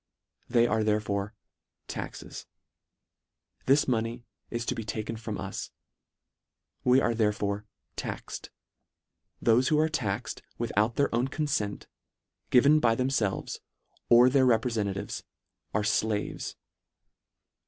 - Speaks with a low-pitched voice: Yes, low, 115 Hz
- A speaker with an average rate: No, slow, 110 wpm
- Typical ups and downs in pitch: Yes, average, 3.2 semitones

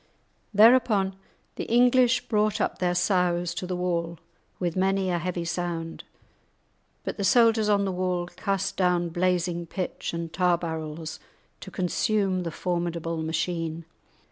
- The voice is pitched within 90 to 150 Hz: No, medium, 180 Hz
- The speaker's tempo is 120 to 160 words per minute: Yes, average, 140 wpm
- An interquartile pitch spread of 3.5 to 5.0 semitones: No, narrow, 2.4 semitones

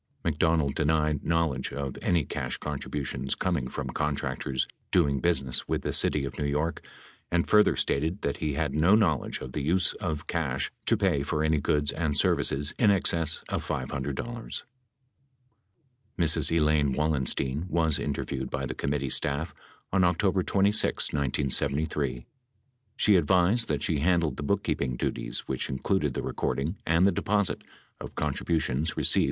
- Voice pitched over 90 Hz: No, very low, 75 Hz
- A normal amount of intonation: Yes, average, 3.5 semitones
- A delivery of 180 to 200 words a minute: No, average, 150 wpm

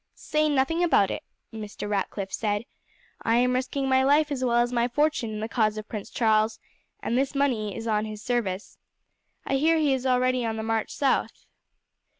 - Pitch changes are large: No, average, 3.7 semitones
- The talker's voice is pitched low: No, high, 240 Hz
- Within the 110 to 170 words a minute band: No, average, 190 wpm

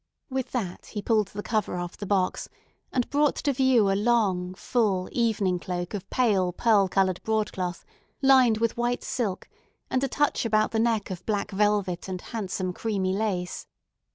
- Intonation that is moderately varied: Yes, average, 3.9 semitones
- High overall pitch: Yes, high, 210 Hz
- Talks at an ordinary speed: Yes, average, 170 wpm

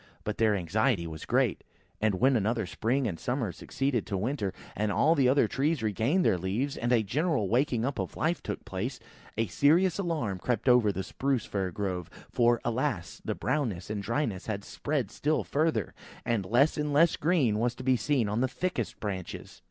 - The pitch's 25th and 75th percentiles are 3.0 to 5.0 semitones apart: No, wide, 5.4 semitones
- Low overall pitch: Yes, low, 120 Hz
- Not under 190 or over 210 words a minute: Yes, average, 200 wpm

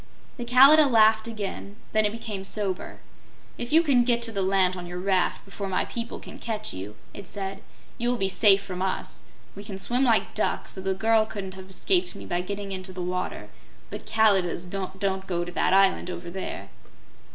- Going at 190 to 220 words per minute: Yes, average, 195 wpm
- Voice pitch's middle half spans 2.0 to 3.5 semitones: Yes, average, 2.9 semitones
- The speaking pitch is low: No, high, 195 Hz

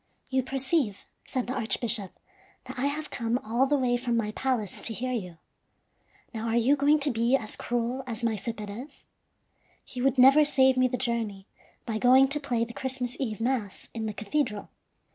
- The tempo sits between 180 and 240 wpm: Yes, average, 185 wpm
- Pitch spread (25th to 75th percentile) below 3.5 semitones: Yes, average, 2.8 semitones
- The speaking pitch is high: Yes, high, 245 Hz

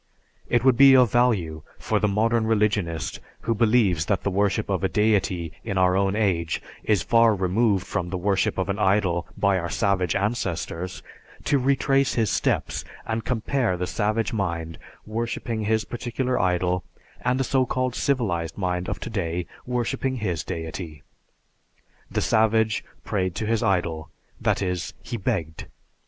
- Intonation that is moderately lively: Yes, average, 4.2 semitones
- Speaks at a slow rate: No, average, 155 wpm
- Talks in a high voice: No, low, 100 Hz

